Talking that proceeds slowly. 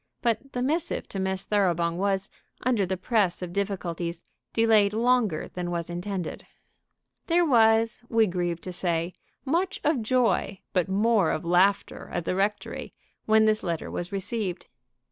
No: average, 150 wpm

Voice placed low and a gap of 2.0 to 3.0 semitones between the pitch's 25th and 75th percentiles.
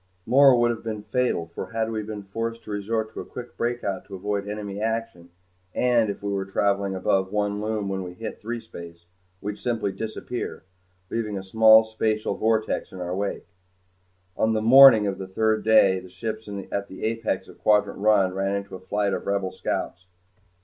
Yes: low, 105 Hz; narrow, 2.4 semitones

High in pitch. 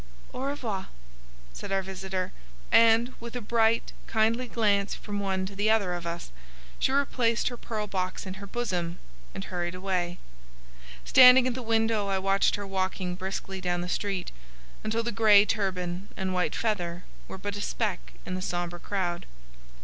Yes: high, 195 Hz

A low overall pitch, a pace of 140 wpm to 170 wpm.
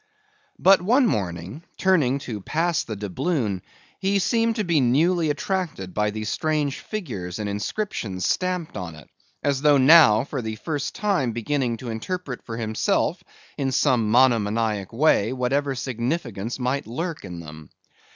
Yes: low, 130 Hz; average, 150 wpm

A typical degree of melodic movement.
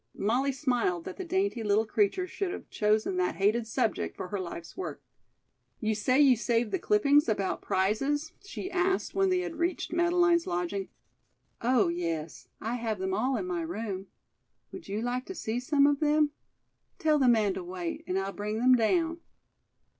No: wide, 8.0 semitones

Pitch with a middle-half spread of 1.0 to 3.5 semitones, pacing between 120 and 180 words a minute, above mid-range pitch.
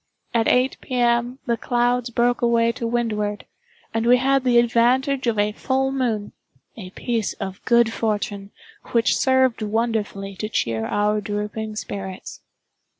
Yes: average, 2.7 semitones; average, 145 wpm; high, 230 Hz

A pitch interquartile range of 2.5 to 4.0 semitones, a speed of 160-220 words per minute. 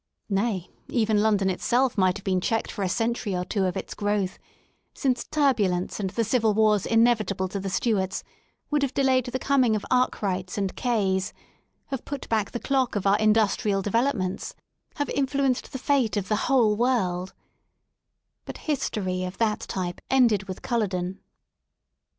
No: average, 4.4 semitones; average, 170 wpm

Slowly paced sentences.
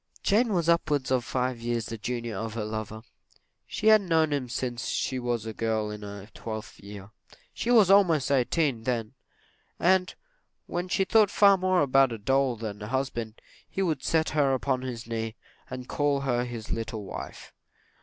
No: average, 180 wpm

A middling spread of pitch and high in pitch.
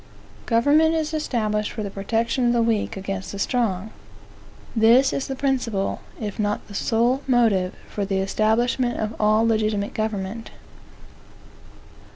Yes: average, 3.0 semitones; high, 220 Hz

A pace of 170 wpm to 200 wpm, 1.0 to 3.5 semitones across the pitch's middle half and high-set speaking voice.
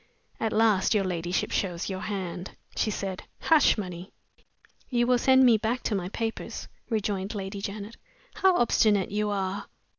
No: average, 155 wpm; average, 3.0 semitones; high, 205 Hz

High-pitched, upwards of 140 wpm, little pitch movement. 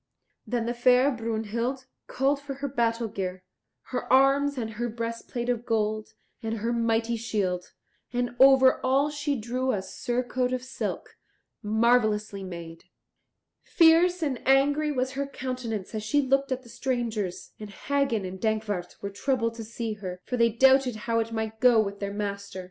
No: high, 235 Hz; average, 165 wpm; average, 3.3 semitones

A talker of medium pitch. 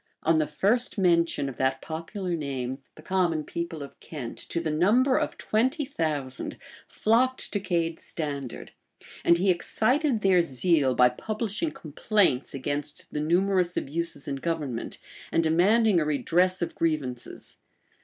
Yes: medium, 170 Hz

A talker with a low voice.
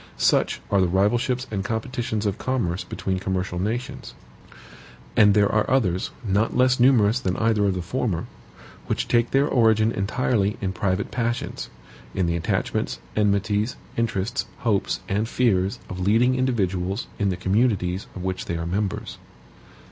Yes: low, 105 Hz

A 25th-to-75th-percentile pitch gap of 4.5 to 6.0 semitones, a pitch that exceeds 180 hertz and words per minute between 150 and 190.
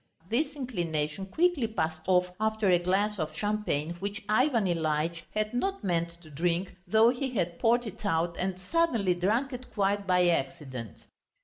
Yes: average, 4.9 semitones; high, 190 Hz; average, 165 wpm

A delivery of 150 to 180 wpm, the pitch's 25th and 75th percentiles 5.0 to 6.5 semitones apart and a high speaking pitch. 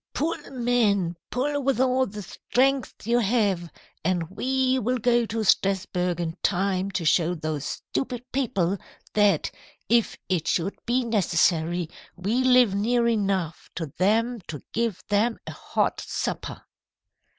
No: average, 140 wpm; average, 5.3 semitones; high, 210 Hz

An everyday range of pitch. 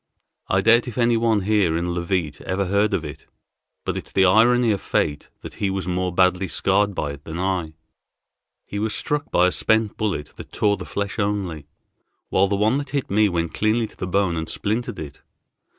Yes: average, 3.5 semitones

